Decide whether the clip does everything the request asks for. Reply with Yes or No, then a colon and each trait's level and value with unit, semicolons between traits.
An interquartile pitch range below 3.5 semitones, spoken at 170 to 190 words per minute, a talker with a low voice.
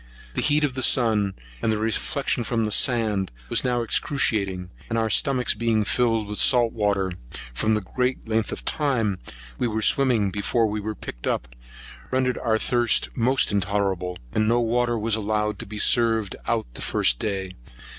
Yes: average, 2.8 semitones; average, 175 wpm; low, 110 Hz